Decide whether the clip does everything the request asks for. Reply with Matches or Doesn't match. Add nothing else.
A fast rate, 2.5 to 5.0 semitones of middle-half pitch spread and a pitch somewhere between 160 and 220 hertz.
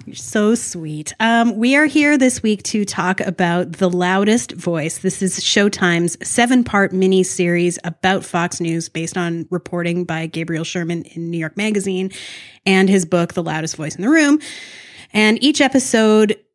Doesn't match